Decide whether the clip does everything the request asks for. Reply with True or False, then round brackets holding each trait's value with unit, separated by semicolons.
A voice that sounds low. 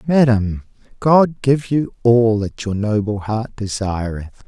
True (115 Hz)